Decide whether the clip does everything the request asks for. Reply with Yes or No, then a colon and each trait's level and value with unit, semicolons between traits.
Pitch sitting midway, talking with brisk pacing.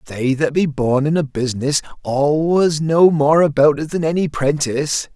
No: medium, 150 Hz; average, 175 wpm